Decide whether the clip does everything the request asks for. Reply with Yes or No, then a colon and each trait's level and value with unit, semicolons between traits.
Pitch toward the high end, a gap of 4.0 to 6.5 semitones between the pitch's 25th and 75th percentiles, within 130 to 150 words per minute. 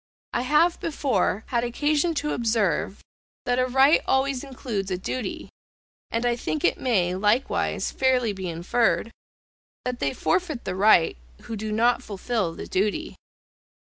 Yes: high, 235 Hz; average, 4.9 semitones; average, 145 wpm